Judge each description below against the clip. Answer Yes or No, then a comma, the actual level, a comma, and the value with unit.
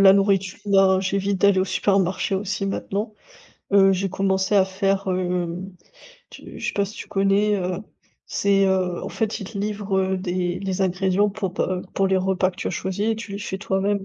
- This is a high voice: Yes, high, 195 Hz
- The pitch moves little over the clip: Yes, narrow, 1.1 semitones